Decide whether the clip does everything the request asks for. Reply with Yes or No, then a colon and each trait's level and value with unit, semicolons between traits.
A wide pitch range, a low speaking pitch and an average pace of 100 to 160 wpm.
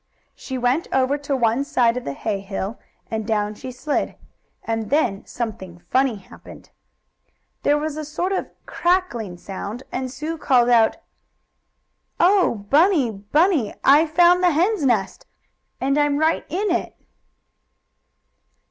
No: wide, 5.9 semitones; very high, 260 Hz; average, 140 wpm